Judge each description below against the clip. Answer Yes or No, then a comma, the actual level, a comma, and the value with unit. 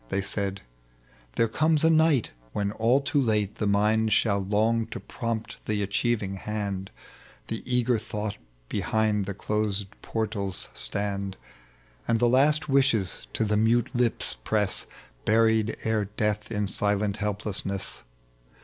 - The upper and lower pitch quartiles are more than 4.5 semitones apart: No, narrow, 2.4 semitones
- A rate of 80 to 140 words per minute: Yes, slow, 135 wpm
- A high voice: No, low, 105 Hz